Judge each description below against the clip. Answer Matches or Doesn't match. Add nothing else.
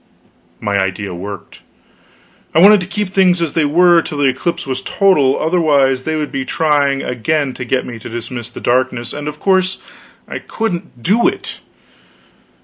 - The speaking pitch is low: Doesn't match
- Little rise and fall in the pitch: Doesn't match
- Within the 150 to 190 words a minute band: Matches